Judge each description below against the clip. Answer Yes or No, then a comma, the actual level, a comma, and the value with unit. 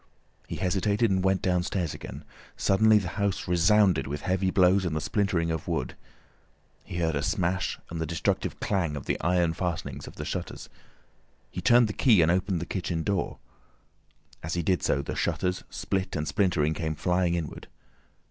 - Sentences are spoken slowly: No, average, 175 wpm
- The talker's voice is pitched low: Yes, very low, 90 Hz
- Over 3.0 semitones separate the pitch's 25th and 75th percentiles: No, average, 2.7 semitones